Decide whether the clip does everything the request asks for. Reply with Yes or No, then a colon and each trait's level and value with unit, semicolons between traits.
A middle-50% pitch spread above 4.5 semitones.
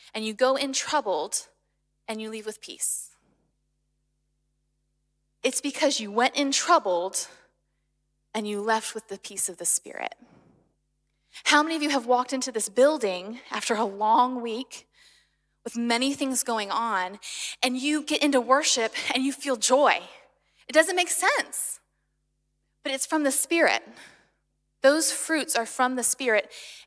No: average, 4.2 semitones